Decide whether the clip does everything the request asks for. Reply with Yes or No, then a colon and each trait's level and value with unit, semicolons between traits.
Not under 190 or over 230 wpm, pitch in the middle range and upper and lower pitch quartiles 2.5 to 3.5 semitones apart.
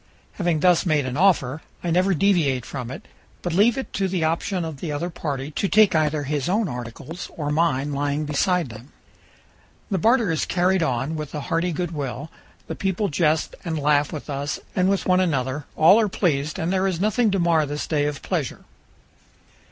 No: average, 200 wpm; medium, 160 Hz; average, 4.0 semitones